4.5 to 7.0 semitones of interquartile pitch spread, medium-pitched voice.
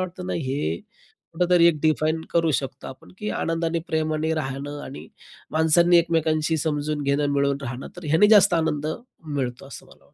No: average, 2.8 semitones; medium, 155 Hz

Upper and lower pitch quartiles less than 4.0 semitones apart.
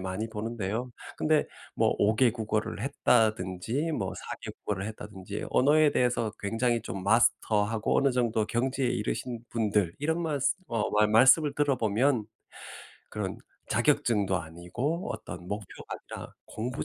Yes: average, 3.6 semitones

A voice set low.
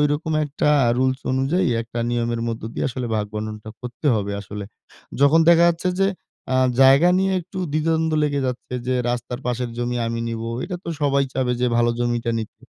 Yes: low, 125 Hz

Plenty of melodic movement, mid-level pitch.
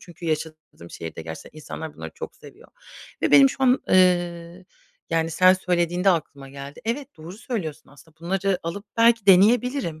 No: average, 4.3 semitones; medium, 175 Hz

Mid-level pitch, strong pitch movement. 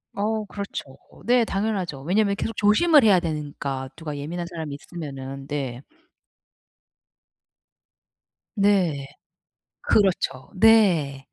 Yes: medium, 175 Hz; wide, 6.5 semitones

